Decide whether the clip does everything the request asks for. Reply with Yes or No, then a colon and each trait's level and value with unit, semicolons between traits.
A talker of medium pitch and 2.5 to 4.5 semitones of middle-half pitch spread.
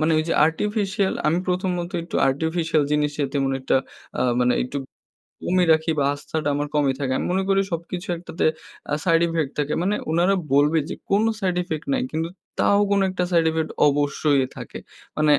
Yes: medium, 160 Hz; average, 3.6 semitones